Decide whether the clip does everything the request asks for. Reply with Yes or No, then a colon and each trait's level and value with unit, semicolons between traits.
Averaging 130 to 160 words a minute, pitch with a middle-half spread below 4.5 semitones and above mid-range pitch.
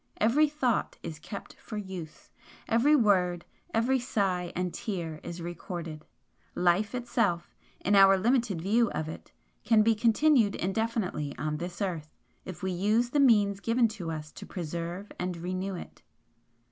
No: average, 150 wpm; average, 4.8 semitones; high, 195 Hz